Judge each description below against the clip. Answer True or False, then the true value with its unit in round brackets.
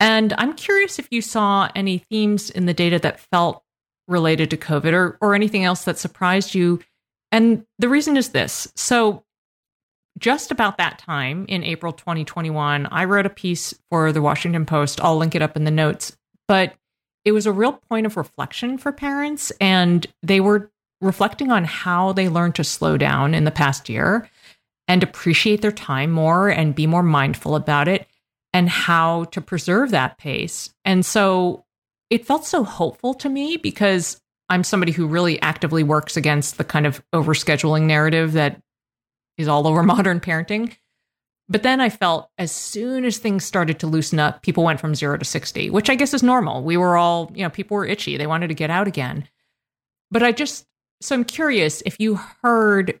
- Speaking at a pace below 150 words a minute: False (190 wpm)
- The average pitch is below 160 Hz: False (180 Hz)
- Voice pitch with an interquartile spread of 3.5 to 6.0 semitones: True (5.0 semitones)